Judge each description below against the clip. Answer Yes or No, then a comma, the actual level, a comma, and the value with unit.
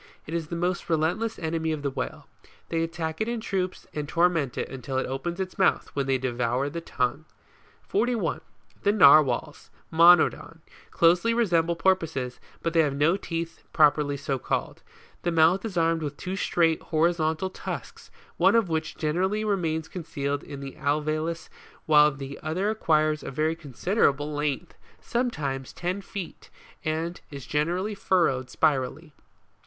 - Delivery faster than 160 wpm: No, average, 155 wpm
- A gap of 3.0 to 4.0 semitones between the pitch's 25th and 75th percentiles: Yes, average, 3.4 semitones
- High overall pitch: No, medium, 160 Hz